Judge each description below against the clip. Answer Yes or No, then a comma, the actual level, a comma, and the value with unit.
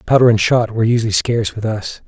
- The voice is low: Yes, low, 115 Hz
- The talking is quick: Yes, fast, 230 wpm